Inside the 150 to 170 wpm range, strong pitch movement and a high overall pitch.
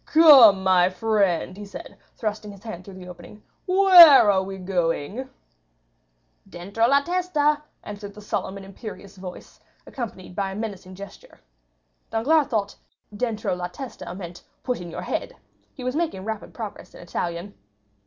No: average, 155 wpm; average, 4.9 semitones; high, 205 Hz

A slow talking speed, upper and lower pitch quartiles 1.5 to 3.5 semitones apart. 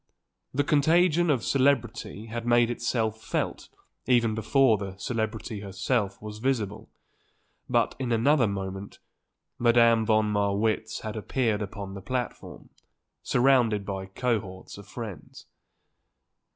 Yes: slow, 115 wpm; average, 3.2 semitones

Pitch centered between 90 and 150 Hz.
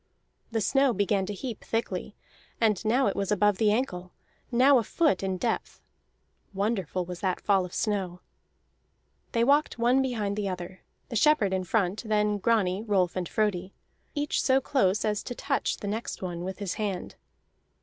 No: high, 205 Hz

